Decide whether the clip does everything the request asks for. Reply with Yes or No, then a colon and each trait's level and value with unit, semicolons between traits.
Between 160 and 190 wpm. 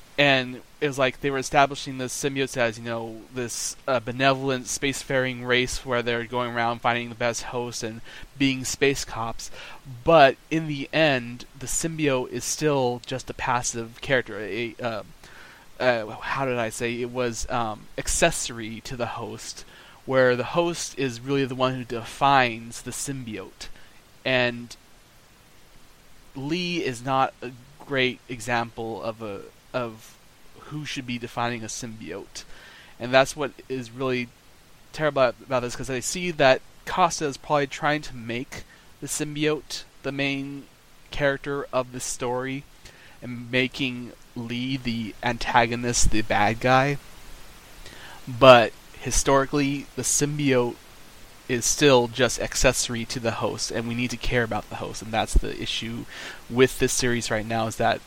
No: average, 150 wpm